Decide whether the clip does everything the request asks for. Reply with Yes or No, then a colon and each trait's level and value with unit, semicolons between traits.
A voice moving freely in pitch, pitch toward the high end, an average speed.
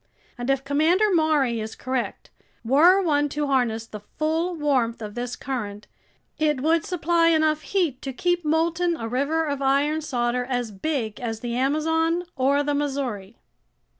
No: average, 4.6 semitones; very high, 285 Hz; average, 160 wpm